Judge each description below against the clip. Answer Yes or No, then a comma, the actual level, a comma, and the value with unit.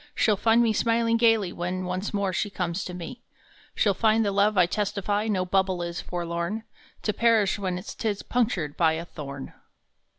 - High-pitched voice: Yes, high, 195 Hz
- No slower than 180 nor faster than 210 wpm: Yes, average, 190 wpm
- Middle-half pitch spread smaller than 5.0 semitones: Yes, average, 3.6 semitones